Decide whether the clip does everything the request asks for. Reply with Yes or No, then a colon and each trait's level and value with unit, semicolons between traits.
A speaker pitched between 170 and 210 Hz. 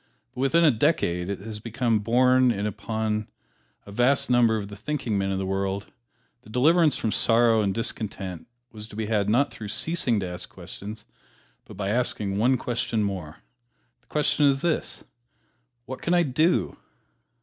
No: low, 110 Hz